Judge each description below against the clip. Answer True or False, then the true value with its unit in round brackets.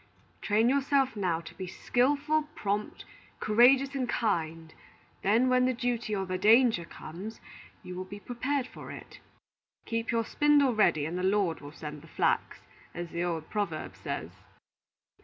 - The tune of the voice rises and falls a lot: True (6.2 semitones)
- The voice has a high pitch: True (215 Hz)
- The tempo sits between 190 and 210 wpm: False (160 wpm)